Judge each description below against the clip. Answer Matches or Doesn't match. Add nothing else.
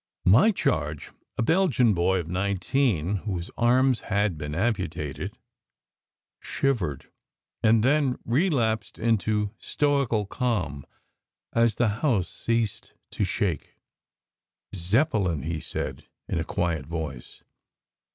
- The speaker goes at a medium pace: Doesn't match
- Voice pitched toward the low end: Matches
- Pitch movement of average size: Doesn't match